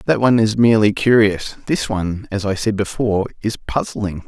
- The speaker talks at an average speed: Yes, average, 185 wpm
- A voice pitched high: No, low, 105 Hz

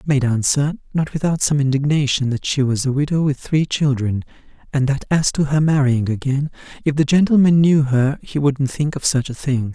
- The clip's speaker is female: No, male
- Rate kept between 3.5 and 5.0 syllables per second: No, 5.3 syllables/s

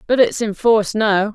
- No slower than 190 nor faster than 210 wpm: No, fast, 225 wpm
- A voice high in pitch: Yes, high, 210 Hz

